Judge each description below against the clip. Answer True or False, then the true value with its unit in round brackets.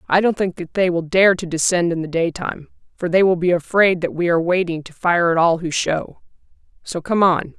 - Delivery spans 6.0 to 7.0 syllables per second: False (5.5 syllables/s)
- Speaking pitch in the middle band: True (175 Hz)